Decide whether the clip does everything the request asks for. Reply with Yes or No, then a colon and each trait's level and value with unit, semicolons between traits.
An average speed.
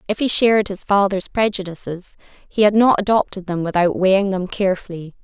Yes: average, 170 wpm